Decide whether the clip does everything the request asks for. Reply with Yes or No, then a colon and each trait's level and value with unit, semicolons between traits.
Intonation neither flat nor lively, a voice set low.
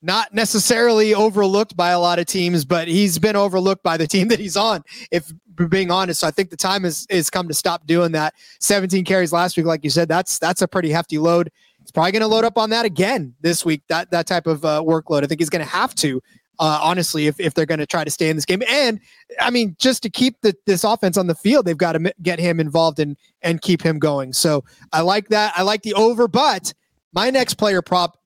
No: average, 4.2 semitones; medium, 180 Hz